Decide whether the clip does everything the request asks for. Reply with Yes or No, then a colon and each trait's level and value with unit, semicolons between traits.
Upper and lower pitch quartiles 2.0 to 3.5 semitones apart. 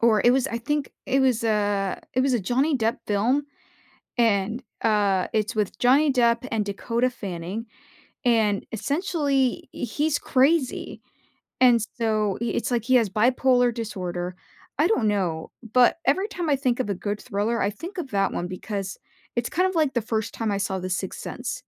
No: average, 4.2 semitones